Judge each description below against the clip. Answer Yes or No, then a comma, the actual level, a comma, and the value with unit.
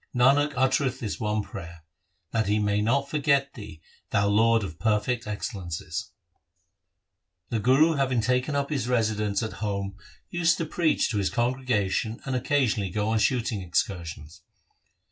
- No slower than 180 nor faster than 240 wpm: No, average, 155 wpm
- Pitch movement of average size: Yes, average, 4.4 semitones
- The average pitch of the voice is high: No, low, 110 Hz